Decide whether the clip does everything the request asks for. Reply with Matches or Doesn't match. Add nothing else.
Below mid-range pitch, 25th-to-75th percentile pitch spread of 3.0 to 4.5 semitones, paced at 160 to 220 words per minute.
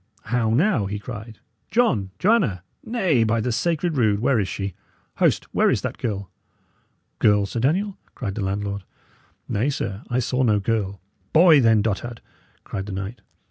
Doesn't match